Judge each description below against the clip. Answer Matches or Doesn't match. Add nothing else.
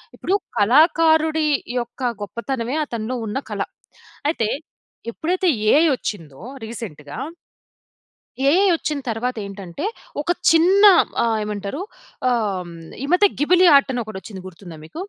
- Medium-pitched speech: Doesn't match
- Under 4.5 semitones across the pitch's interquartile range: Doesn't match